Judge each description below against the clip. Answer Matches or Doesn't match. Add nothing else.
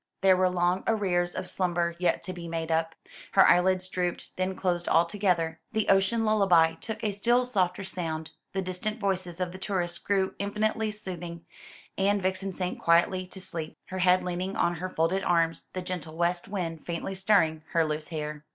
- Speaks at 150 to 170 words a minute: Doesn't match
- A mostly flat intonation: Matches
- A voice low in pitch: Doesn't match